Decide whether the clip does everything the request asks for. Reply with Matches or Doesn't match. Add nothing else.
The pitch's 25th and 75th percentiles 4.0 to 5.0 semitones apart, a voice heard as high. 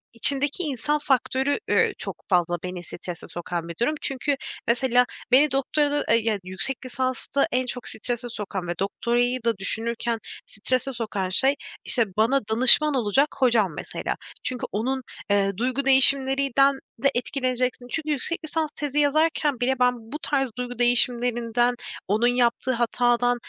Doesn't match